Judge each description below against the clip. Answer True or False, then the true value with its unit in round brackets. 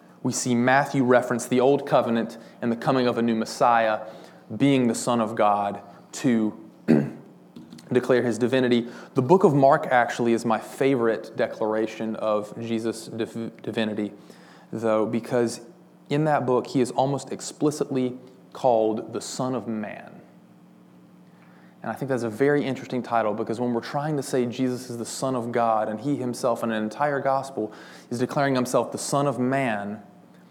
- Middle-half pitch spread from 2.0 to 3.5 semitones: True (2.9 semitones)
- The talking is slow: False (165 wpm)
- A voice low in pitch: True (120 Hz)